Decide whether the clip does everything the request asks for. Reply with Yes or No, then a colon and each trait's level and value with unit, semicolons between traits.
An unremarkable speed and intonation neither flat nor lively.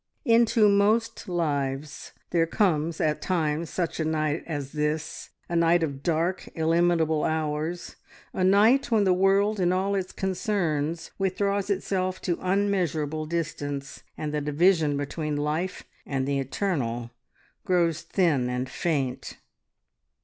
No: slow, 130 wpm; average, 4.0 semitones